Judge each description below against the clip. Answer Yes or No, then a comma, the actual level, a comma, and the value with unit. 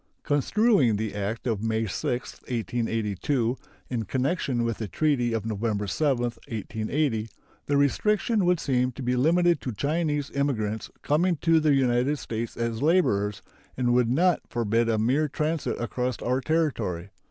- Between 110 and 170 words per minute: Yes, average, 150 wpm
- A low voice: Yes, low, 125 Hz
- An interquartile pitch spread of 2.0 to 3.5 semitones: No, average, 4.8 semitones